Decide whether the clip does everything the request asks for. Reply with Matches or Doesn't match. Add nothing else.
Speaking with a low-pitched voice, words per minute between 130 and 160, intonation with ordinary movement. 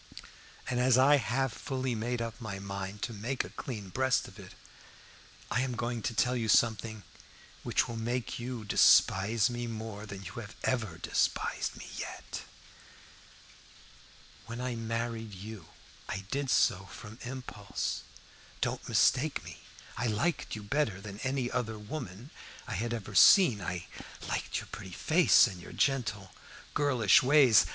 Matches